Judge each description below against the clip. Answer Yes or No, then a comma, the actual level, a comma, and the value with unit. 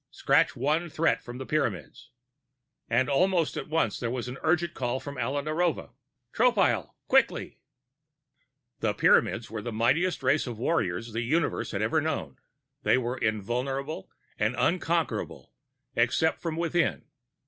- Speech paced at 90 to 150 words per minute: Yes, average, 140 wpm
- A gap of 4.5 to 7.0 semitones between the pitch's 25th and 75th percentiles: Yes, average, 5.3 semitones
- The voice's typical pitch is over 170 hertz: No, low, 135 Hz